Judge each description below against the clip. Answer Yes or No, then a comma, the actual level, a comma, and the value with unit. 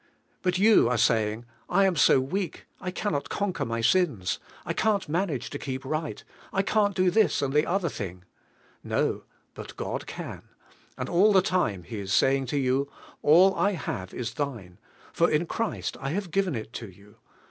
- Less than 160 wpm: No, average, 195 wpm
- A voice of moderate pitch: Yes, medium, 145 Hz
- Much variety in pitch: Yes, wide, 8.2 semitones